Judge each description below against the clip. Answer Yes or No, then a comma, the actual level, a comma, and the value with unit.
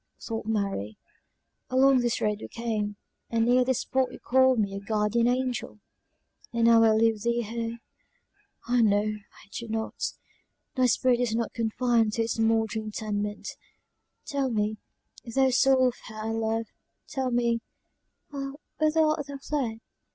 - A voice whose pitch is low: No, high, 230 Hz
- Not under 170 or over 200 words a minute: No, average, 155 wpm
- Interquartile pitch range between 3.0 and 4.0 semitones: No, narrow, 2.6 semitones